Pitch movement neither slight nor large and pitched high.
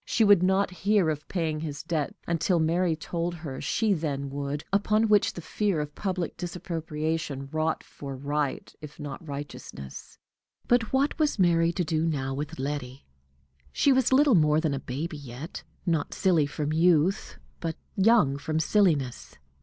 No: average, 4.0 semitones; medium, 160 Hz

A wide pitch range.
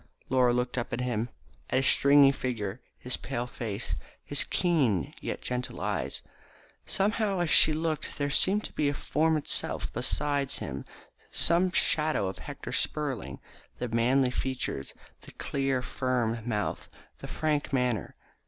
No: average, 3.9 semitones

